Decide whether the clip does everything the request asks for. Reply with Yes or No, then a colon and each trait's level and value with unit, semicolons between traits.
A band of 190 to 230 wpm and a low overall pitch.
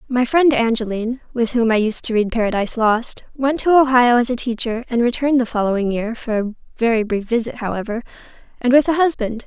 No: average, 195 wpm; high, 235 Hz